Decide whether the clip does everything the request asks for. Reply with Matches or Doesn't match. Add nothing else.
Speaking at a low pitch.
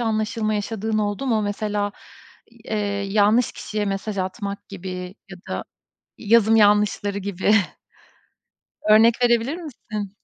Doesn't match